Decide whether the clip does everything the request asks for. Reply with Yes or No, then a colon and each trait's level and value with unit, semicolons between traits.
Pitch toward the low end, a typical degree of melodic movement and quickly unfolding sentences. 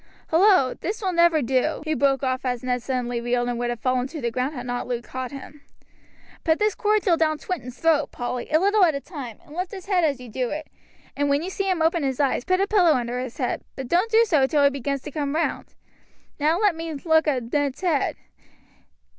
No: very high, 290 Hz; average, 5.0 semitones; fast, 235 wpm